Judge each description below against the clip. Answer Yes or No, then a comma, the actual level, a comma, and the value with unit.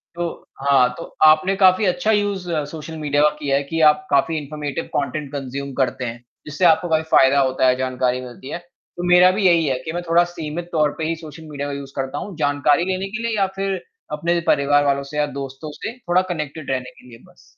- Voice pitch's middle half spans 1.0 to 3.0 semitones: No, average, 3.9 semitones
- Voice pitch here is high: No, medium, 150 Hz